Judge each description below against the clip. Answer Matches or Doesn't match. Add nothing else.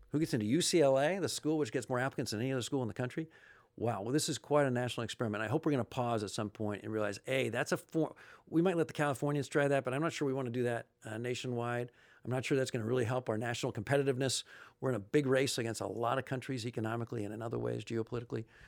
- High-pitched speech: Doesn't match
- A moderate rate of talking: Doesn't match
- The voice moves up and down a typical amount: Matches